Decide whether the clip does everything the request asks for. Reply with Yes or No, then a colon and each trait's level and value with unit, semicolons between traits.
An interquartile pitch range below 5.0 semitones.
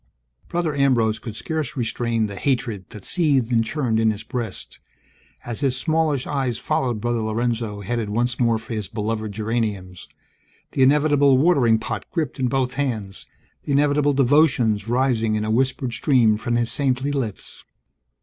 Yes: average, 3.8 semitones